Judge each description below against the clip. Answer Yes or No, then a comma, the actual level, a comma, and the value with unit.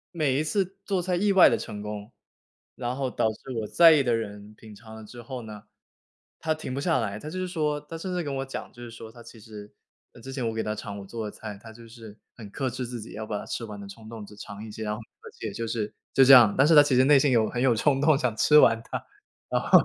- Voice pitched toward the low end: Yes, low, 120 Hz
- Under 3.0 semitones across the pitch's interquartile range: No, average, 4.7 semitones